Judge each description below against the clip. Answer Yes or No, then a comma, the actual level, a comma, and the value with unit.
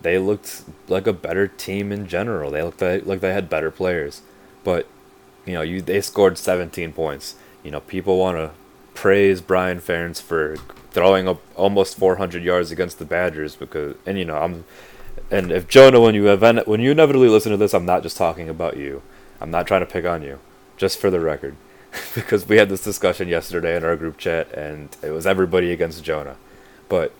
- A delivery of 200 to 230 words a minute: Yes, fast, 205 wpm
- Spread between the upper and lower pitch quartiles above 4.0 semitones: No, average, 3.6 semitones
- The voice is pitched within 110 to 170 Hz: No, very low, 95 Hz